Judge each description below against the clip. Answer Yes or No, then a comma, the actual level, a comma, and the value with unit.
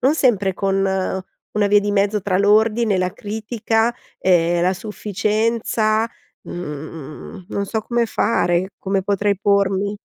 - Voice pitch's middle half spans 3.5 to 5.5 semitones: No, narrow, 2.4 semitones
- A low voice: No, high, 205 Hz